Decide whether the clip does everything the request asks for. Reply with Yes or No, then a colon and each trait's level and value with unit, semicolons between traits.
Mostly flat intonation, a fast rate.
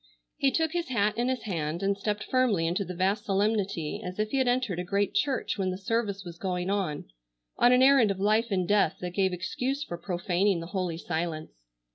No: average, 4.2 semitones; fast, 215 wpm